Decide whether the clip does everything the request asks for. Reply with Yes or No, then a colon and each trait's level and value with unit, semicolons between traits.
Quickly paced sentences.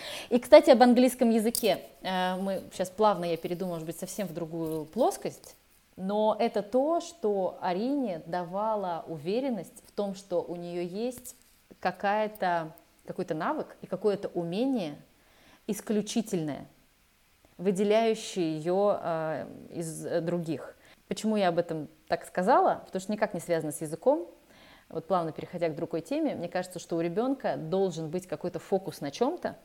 No: average, 140 wpm